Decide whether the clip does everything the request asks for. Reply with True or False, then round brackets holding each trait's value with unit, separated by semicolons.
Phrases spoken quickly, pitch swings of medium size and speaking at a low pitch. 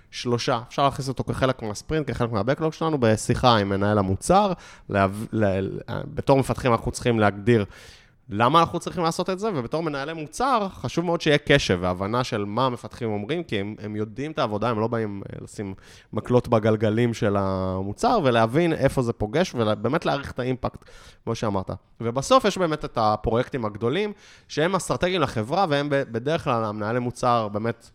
True (165 wpm; 5.0 semitones; 120 Hz)